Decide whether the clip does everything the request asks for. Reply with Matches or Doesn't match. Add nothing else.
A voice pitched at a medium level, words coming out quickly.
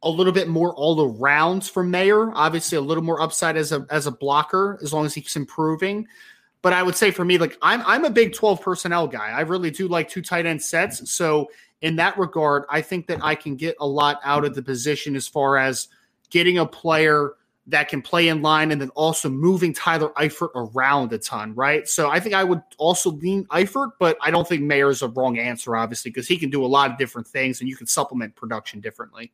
Matches